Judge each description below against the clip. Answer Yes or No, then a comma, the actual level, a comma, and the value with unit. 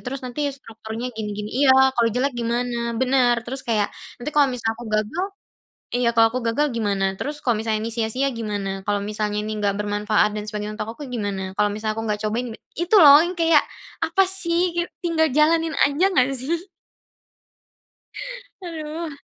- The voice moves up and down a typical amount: No, wide, 5.8 semitones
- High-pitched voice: Yes, high, 240 Hz